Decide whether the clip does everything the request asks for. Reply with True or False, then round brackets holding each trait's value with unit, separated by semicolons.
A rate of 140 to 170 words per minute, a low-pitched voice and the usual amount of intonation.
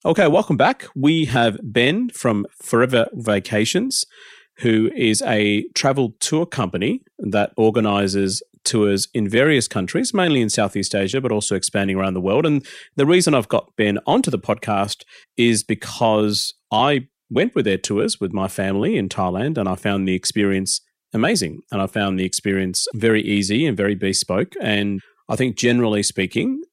True (165 wpm; 105 Hz; 3.8 semitones)